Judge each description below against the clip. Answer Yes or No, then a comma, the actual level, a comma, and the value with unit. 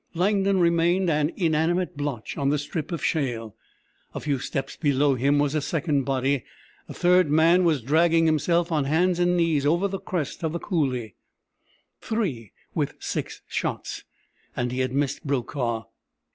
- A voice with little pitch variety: No, average, 3.9 semitones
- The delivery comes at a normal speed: Yes, average, 160 wpm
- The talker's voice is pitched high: No, medium, 150 Hz